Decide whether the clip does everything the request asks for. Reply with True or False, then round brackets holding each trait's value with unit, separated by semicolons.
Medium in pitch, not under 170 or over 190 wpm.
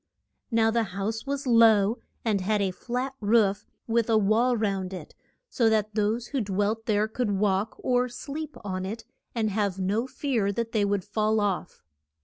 False (215 Hz; 175 wpm)